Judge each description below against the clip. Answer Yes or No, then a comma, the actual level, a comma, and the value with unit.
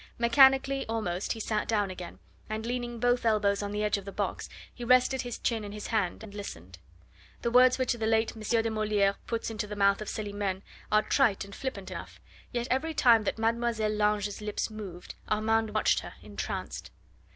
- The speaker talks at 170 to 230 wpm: Yes, average, 195 wpm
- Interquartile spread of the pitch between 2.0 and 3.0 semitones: Yes, narrow, 2.5 semitones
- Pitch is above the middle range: Yes, high, 215 Hz